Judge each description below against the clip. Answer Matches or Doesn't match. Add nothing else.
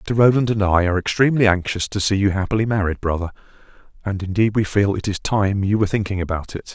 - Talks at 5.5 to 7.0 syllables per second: Matches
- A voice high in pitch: Doesn't match